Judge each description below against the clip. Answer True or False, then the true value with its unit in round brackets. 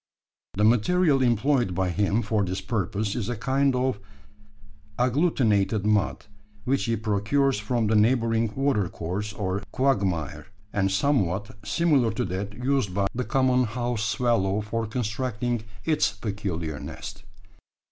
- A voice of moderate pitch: False (110 Hz)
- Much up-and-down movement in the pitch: False (4.0 semitones)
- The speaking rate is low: True (130 wpm)